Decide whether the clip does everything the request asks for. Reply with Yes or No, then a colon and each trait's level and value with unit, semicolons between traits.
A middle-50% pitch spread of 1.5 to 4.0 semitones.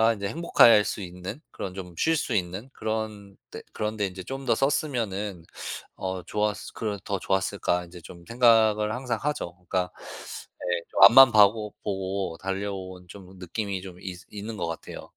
Yes: average, 2.9 semitones